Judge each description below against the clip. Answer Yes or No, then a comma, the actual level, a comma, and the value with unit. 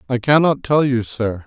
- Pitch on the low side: Yes, low, 125 Hz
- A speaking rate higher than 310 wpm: No, fast, 205 wpm